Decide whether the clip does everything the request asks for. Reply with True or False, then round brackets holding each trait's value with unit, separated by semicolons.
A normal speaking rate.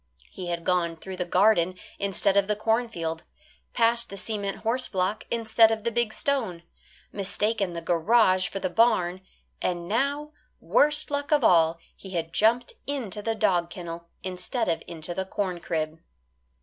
True (160 wpm)